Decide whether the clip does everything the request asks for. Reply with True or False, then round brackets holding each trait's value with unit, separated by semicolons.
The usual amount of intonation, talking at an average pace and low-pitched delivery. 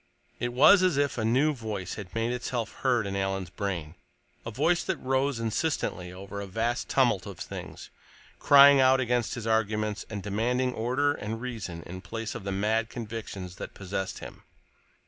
True (4.4 semitones; 180 wpm; 115 Hz)